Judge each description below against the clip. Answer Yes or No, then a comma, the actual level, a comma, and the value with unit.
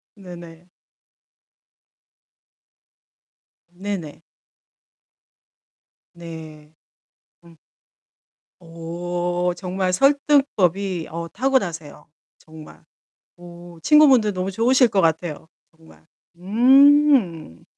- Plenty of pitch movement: No, average, 4.4 semitones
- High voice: No, medium, 175 Hz